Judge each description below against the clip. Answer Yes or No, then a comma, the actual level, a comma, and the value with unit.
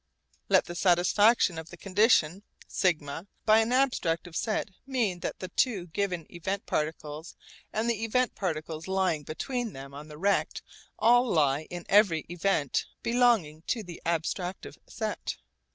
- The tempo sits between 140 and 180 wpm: Yes, average, 145 wpm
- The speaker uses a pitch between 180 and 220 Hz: Yes, medium, 185 Hz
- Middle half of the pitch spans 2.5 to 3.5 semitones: No, wide, 5.4 semitones